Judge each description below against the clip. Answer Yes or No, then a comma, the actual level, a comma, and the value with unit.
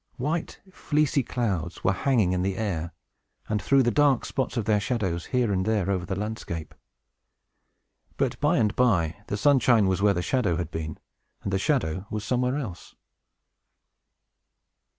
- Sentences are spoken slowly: No, average, 160 wpm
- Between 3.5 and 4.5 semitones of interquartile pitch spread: No, wide, 5.4 semitones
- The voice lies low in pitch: Yes, low, 105 Hz